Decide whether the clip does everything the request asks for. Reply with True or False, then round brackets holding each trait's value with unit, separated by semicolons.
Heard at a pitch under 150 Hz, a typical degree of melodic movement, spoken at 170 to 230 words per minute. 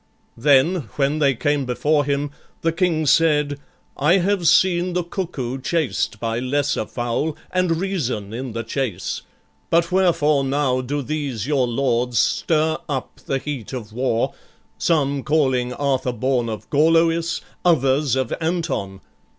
False (140 Hz; 4.5 semitones; 140 wpm)